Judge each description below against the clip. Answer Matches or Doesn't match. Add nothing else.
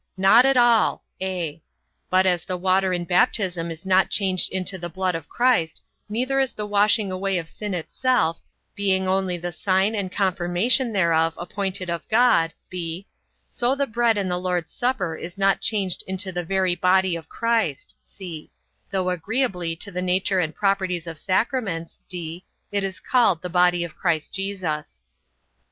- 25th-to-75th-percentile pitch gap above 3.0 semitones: Doesn't match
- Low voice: Doesn't match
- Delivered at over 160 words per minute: Matches